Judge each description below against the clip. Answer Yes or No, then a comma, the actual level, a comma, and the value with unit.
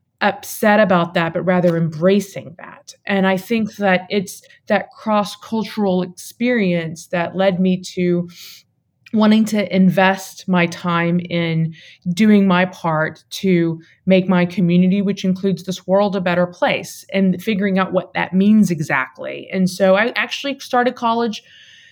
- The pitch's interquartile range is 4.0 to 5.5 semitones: No, average, 2.7 semitones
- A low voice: No, high, 190 Hz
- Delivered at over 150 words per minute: No, average, 145 wpm